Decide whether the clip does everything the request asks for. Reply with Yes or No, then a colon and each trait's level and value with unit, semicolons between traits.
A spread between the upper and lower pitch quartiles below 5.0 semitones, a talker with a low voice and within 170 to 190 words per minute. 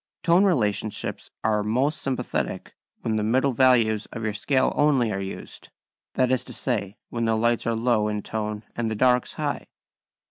Yes: average, 3.2 semitones; low, 115 Hz; average, 175 wpm